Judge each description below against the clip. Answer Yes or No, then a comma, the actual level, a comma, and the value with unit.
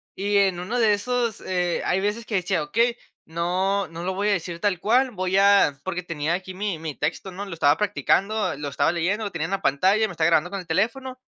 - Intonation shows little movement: No, average, 3.4 semitones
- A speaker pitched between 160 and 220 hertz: Yes, high, 190 Hz